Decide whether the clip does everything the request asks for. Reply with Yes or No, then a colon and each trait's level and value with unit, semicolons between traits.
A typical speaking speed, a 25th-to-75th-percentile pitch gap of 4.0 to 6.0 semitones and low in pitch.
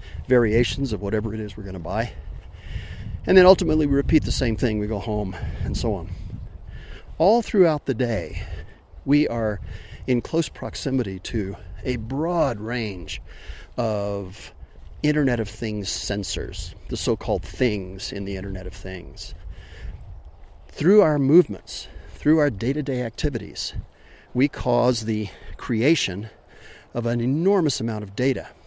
Yes: average, 145 wpm; wide, 5.4 semitones; low, 110 Hz